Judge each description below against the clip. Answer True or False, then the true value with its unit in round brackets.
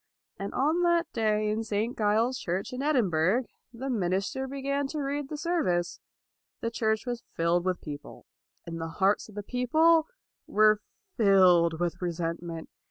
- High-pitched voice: True (215 Hz)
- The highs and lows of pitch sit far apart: True (7.1 semitones)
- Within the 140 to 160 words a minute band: True (155 wpm)